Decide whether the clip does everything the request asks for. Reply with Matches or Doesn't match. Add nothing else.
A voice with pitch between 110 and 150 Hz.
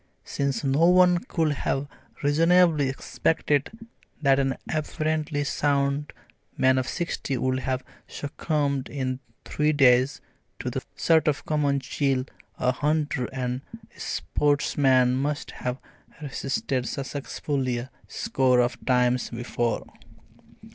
Matches